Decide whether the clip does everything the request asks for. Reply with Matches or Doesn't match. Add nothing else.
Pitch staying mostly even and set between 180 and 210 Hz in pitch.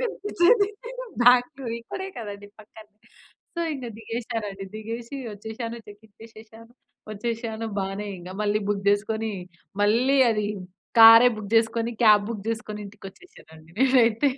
Doesn't match